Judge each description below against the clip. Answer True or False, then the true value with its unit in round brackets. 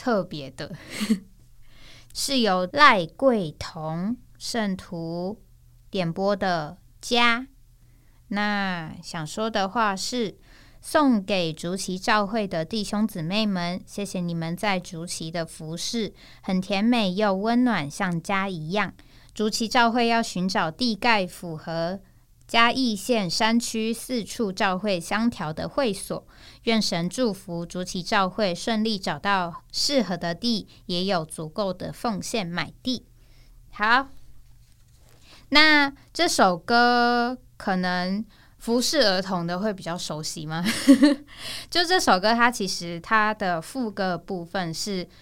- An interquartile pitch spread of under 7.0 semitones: True (5.1 semitones)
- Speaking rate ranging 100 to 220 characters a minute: True (180 characters per minute)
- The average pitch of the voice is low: False (195 Hz)